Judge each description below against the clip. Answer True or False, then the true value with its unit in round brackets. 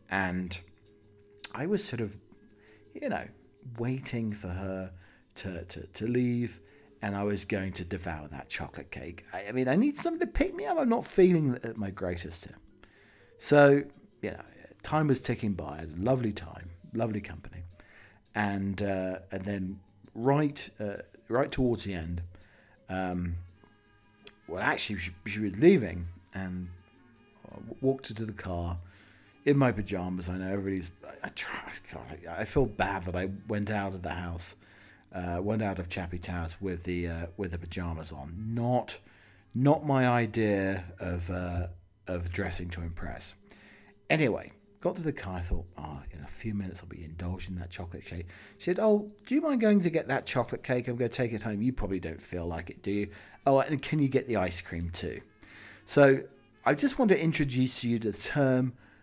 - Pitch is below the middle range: True (100 Hz)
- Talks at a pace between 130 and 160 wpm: False (185 wpm)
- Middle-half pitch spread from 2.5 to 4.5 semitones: False (5.3 semitones)